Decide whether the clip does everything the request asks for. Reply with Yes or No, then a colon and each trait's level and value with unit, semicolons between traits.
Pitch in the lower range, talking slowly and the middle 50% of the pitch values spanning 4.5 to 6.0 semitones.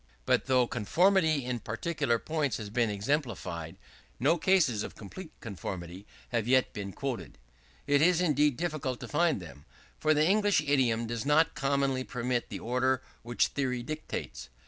No: low, 130 Hz; average, 155 wpm; average, 5.2 semitones